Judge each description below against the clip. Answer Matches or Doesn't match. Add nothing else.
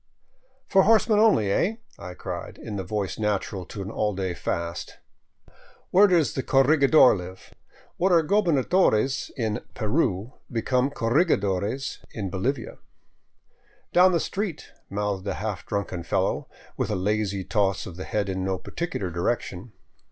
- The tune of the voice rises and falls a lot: Matches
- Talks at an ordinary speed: Matches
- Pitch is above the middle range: Doesn't match